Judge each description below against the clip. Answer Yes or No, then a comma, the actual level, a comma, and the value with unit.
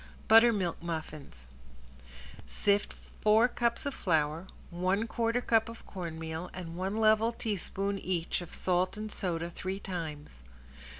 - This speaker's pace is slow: Yes, slow, 125 wpm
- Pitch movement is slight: No, average, 4.6 semitones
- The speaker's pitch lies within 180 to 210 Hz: Yes, medium, 185 Hz